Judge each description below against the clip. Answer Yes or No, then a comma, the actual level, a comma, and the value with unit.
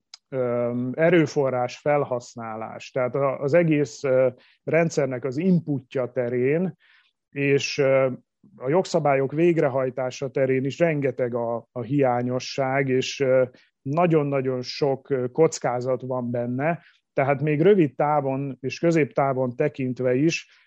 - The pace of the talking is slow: Yes, slow, 95 wpm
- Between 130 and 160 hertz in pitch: Yes, low, 135 Hz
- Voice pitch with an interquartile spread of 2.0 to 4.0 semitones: Yes, average, 2.8 semitones